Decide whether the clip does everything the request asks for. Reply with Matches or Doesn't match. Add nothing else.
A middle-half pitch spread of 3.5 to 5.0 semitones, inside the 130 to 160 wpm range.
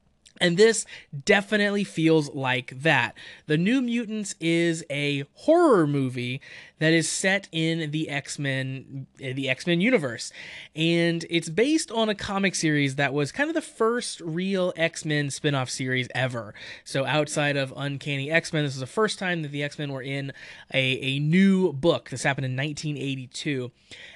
Matches